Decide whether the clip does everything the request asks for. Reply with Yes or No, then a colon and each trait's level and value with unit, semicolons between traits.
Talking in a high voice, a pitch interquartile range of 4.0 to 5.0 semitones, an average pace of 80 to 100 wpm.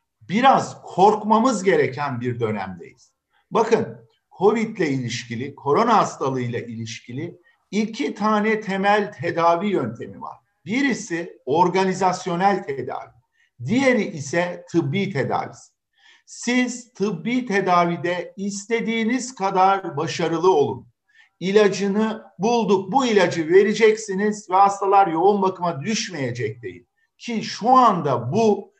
Yes: high, 200 Hz; average, 4.6 semitones; slow, 95 wpm